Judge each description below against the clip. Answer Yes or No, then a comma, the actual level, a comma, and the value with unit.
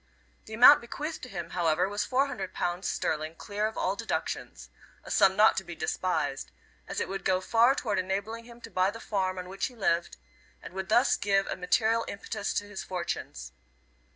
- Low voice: No, high, 195 Hz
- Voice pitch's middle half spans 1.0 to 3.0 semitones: No, average, 3.6 semitones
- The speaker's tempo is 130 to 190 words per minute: No, average, 200 wpm